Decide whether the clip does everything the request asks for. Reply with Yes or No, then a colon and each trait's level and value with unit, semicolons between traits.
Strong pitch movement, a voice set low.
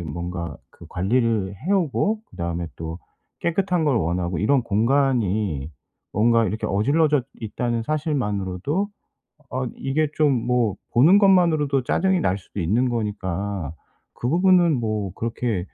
Yes: wide, 7.5 semitones; low, 115 Hz